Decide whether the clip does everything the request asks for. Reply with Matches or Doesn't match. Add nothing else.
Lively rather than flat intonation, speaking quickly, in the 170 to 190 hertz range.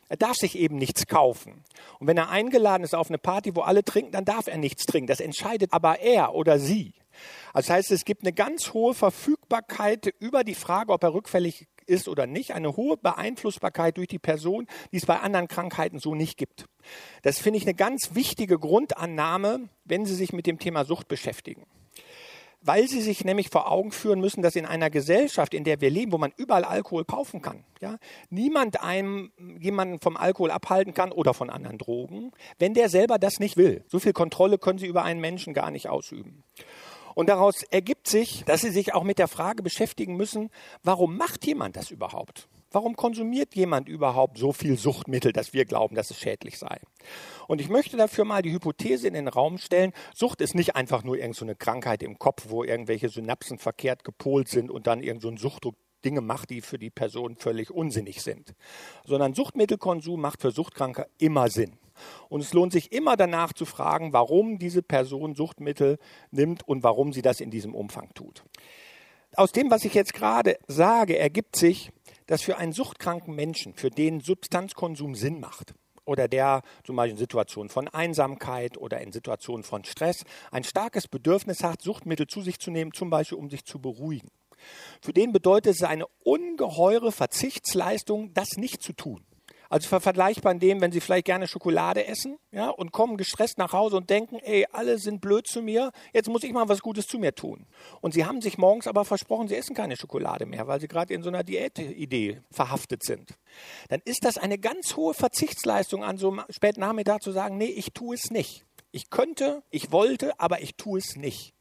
Matches